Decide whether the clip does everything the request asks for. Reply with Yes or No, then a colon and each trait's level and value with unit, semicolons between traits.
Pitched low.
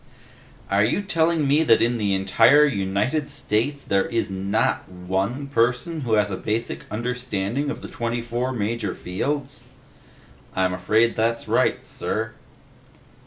Yes: low, 115 Hz